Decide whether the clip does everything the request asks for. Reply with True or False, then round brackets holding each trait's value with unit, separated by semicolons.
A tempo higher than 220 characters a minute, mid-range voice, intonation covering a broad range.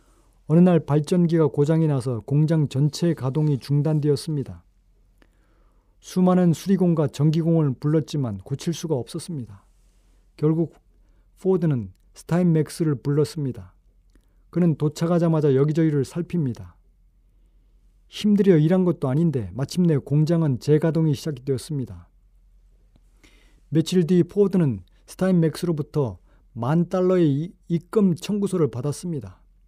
True (285 characters per minute; 150 Hz; 7.0 semitones)